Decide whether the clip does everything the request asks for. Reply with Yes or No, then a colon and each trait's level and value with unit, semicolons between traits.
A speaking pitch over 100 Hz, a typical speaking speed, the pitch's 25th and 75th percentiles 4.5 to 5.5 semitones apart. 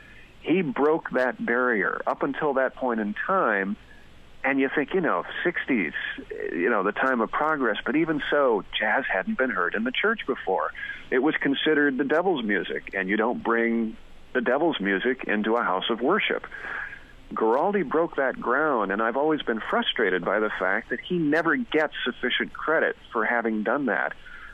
Yes: low, 135 Hz; average, 180 wpm; average, 5.1 semitones